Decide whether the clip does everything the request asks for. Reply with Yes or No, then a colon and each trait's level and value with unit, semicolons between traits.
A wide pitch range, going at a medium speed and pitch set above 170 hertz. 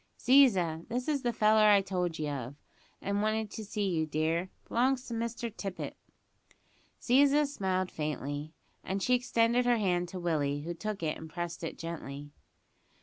Yes: wide, 6.3 semitones; average, 165 wpm; high, 190 Hz